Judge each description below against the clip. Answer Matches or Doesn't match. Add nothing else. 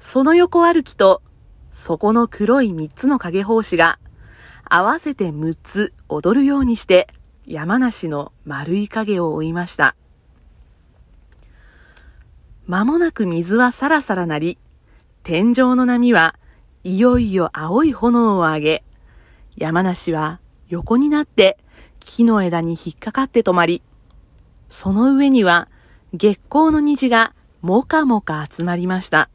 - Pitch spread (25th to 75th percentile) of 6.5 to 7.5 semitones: Matches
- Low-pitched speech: Doesn't match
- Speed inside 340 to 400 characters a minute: Doesn't match